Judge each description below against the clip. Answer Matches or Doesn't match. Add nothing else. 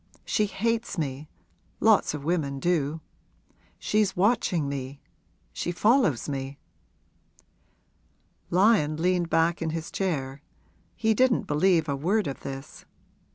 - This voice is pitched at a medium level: Matches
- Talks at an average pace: Doesn't match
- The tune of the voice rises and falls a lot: Matches